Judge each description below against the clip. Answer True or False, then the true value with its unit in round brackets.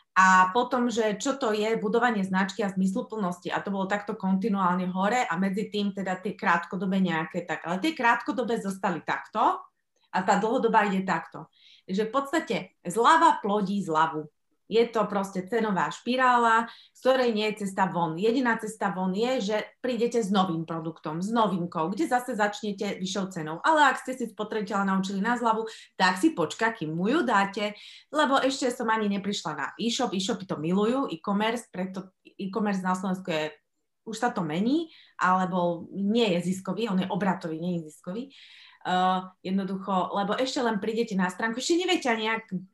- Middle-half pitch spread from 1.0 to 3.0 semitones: False (4.0 semitones)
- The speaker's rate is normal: False (175 wpm)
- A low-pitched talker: False (205 Hz)